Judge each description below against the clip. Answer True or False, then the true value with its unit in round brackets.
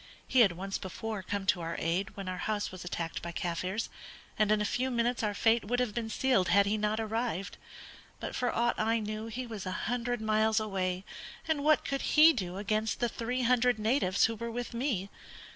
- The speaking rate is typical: False (210 wpm)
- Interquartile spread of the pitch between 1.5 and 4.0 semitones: True (3.5 semitones)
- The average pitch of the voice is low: False (215 Hz)